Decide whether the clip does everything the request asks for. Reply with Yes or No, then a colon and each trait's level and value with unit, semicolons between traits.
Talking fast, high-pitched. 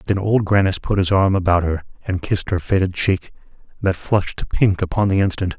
No: fast, 215 wpm; very low, 95 Hz